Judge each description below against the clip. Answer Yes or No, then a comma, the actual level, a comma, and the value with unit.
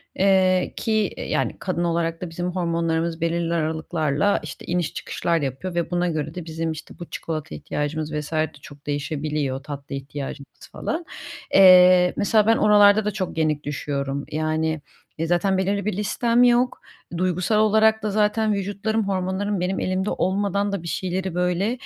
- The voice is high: No, medium, 175 Hz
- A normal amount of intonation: Yes, average, 4.2 semitones